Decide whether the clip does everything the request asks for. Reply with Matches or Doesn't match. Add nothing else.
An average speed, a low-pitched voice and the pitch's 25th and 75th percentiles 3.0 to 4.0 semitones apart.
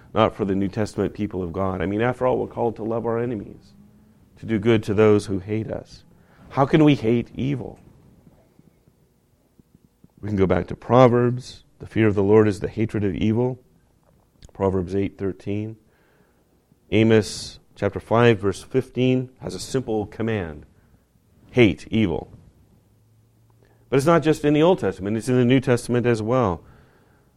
Matches